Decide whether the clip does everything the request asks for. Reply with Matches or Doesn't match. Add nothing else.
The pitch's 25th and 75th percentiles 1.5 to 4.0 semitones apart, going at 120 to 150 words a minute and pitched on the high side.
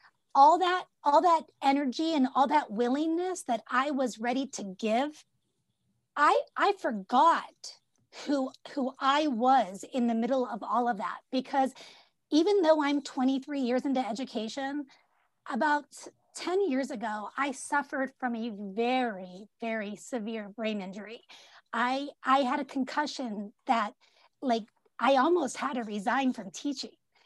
Matches